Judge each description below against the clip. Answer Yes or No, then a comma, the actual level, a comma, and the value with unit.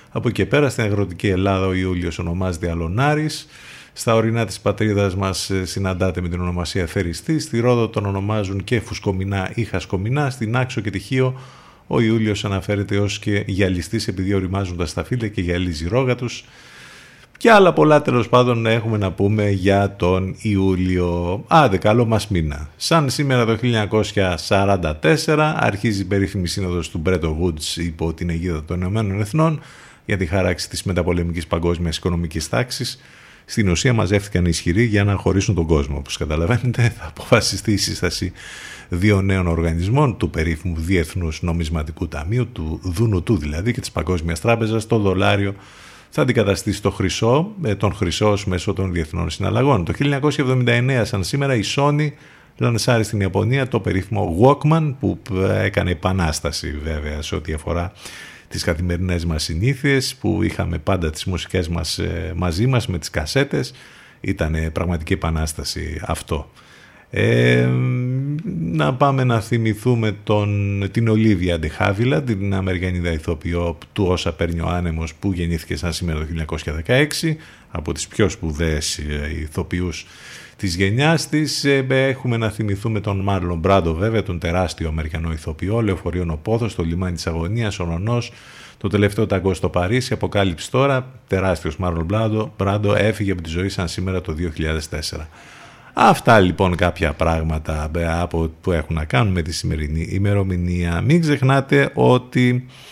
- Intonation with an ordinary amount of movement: Yes, average, 4.7 semitones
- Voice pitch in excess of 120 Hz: No, very low, 95 Hz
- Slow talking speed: No, average, 150 wpm